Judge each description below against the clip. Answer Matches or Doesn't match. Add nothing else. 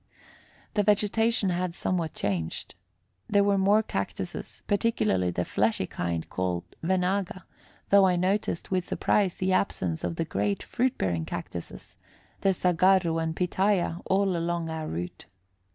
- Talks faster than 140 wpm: Doesn't match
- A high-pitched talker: Doesn't match